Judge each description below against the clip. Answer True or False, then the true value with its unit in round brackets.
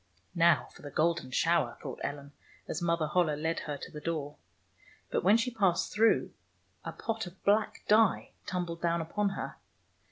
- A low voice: False (170 Hz)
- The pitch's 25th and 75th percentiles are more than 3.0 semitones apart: True (4.5 semitones)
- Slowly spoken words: False (170 wpm)